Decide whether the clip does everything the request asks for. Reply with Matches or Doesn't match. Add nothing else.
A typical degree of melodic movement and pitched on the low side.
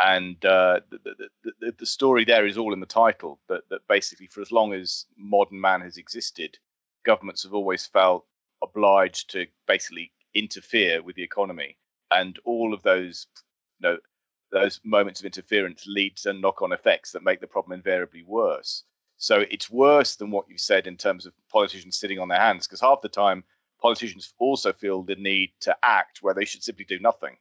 Matches